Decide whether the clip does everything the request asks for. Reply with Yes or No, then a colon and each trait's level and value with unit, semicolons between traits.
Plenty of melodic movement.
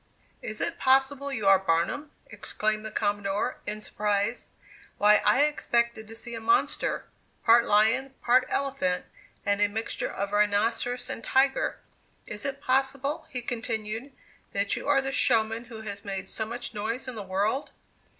No: average, 4.1 semitones